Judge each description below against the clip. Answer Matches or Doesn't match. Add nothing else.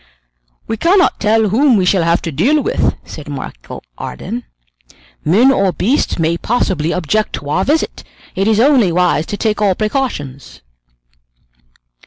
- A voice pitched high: Matches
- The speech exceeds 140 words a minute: Matches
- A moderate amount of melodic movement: Doesn't match